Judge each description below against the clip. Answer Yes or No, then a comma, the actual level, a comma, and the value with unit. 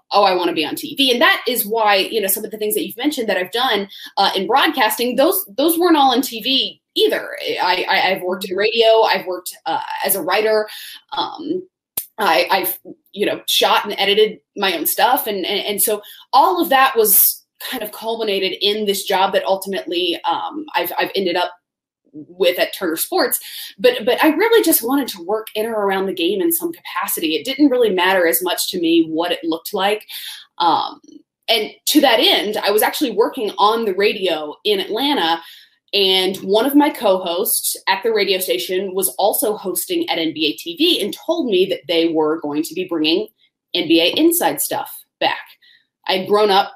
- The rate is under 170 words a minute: No, average, 200 wpm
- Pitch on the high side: Yes, high, 220 Hz